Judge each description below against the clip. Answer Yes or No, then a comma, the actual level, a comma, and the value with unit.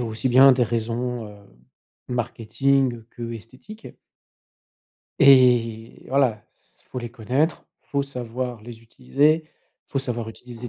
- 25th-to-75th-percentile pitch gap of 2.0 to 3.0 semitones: Yes, narrow, 2.6 semitones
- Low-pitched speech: Yes, low, 120 Hz